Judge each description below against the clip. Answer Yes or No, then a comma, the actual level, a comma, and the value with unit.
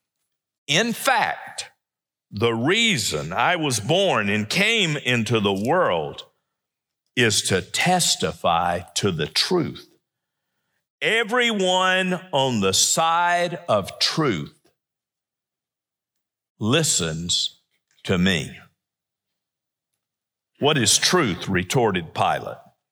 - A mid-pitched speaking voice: Yes, medium, 165 Hz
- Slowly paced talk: Yes, slow, 85 wpm